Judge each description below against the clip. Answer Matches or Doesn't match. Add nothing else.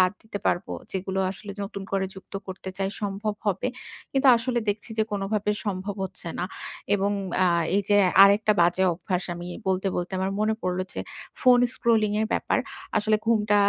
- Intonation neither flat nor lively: Doesn't match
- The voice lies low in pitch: Doesn't match